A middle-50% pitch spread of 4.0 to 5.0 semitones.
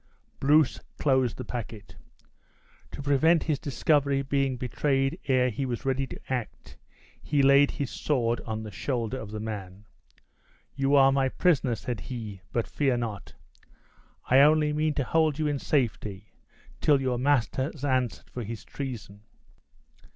No: average, 3.3 semitones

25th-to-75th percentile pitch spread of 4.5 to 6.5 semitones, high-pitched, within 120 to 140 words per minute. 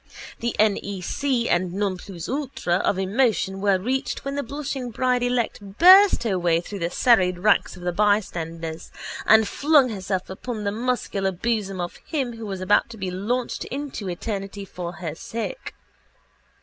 No: average, 4.8 semitones; high, 205 Hz; average, 160 wpm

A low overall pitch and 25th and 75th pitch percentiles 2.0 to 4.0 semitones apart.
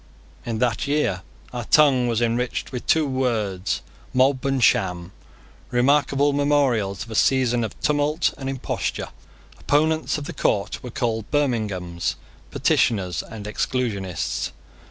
No: low, 125 Hz; average, 5.0 semitones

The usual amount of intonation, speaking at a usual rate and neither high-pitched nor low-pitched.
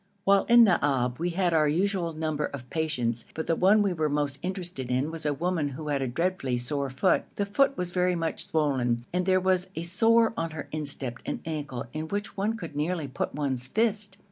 No: average, 4.8 semitones; fast, 215 wpm; medium, 160 Hz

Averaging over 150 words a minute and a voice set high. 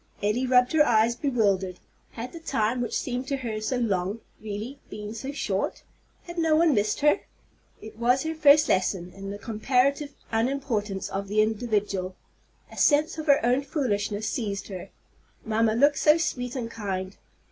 Yes: average, 170 wpm; high, 230 Hz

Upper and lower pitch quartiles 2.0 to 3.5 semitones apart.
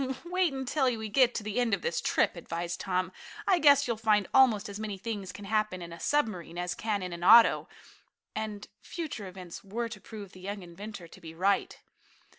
No: average, 4.1 semitones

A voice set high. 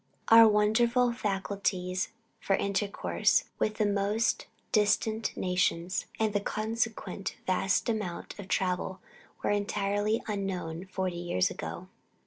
Yes: high, 200 Hz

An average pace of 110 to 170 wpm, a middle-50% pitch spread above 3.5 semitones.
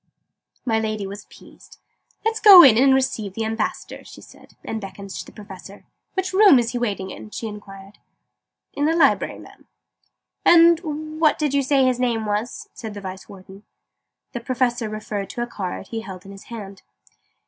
No: average, 180 wpm; average, 5.2 semitones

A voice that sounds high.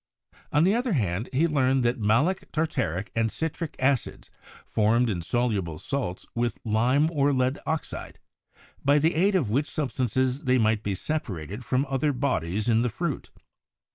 No: low, 130 Hz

